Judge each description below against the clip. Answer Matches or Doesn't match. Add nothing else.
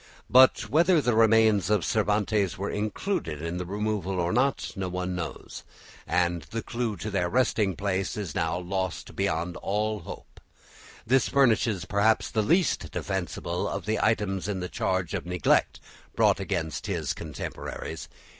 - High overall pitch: Doesn't match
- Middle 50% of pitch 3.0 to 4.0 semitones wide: Matches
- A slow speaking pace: Doesn't match